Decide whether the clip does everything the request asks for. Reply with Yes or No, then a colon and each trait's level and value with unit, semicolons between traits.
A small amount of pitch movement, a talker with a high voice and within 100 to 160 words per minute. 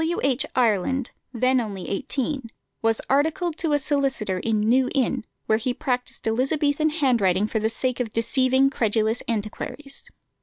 No: average, 3.7 semitones; very high, 250 Hz; average, 150 wpm